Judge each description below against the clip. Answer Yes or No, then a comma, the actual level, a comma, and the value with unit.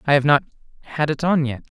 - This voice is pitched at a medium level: Yes, medium, 145 Hz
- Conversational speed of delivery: No, fast, 235 wpm